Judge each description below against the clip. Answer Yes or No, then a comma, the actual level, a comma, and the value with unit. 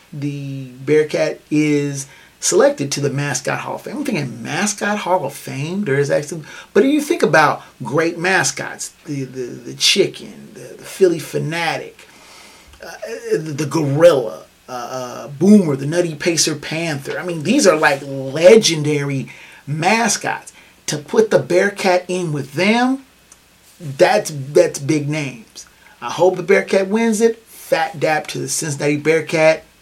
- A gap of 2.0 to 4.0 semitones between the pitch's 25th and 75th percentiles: No, average, 4.6 semitones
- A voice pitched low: No, medium, 160 Hz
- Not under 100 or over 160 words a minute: Yes, average, 150 wpm